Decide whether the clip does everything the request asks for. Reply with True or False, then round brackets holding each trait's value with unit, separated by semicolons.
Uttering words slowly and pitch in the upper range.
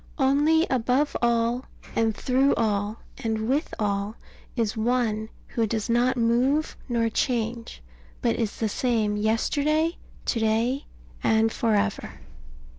True (125 wpm; 230 Hz)